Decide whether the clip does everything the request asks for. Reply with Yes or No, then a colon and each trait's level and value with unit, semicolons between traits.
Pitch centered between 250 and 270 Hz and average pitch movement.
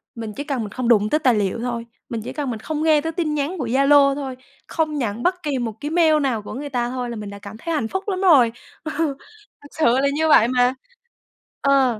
Yes: very high, 265 Hz; average, 4.6 semitones